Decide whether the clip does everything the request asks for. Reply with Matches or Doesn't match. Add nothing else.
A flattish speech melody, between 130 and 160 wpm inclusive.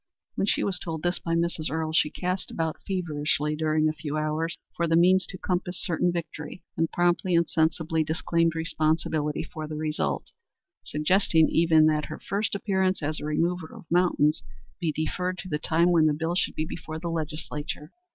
Doesn't match